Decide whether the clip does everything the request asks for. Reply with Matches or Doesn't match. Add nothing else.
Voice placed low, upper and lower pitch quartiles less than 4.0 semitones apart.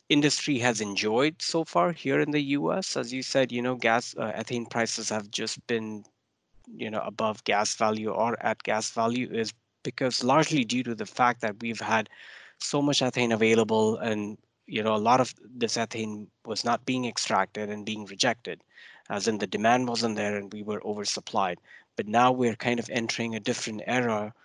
Matches